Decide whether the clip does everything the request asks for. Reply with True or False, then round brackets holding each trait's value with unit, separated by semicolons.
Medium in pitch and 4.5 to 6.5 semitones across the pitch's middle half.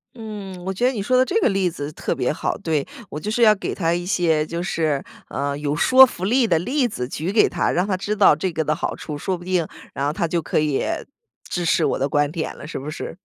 True (175 Hz; 5.1 semitones)